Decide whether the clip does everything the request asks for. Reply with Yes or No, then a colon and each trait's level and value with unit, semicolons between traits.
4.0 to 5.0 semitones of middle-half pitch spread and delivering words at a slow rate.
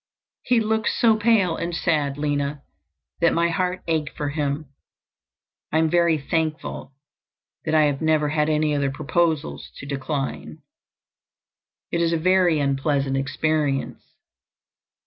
No: average, 2.9 semitones; slow, 130 wpm